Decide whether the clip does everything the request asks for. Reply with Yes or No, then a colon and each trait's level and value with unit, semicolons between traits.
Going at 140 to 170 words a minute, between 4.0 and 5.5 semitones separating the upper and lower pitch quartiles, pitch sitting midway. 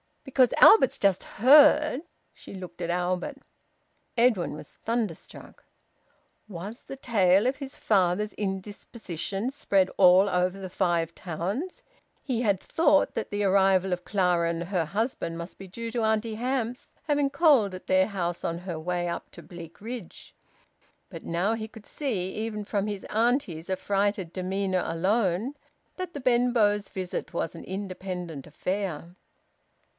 No: average, 145 wpm; average, 4.5 semitones; high, 195 Hz